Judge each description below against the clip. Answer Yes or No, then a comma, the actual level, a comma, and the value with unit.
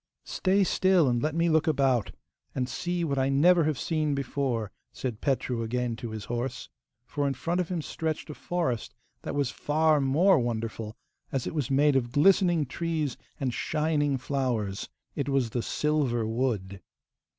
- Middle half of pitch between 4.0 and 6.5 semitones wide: Yes, average, 4.5 semitones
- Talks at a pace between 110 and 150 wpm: No, average, 170 wpm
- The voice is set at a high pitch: No, medium, 140 Hz